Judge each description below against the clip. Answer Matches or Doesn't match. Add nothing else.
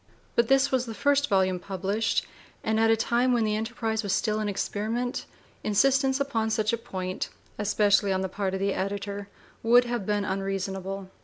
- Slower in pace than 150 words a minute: Doesn't match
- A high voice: Matches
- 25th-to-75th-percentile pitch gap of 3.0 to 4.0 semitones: Matches